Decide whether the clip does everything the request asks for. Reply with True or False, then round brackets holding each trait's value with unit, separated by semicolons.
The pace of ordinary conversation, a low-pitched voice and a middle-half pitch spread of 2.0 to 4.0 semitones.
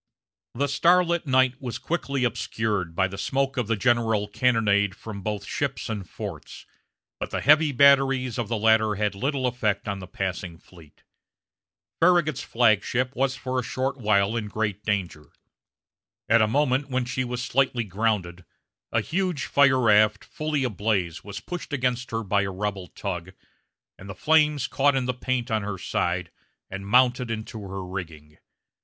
False (165 wpm; 115 Hz; 4.6 semitones)